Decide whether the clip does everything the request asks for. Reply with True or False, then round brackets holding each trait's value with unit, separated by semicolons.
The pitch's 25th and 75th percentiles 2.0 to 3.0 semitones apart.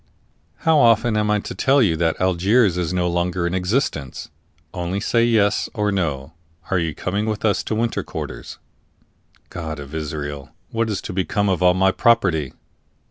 False (4.3 semitones)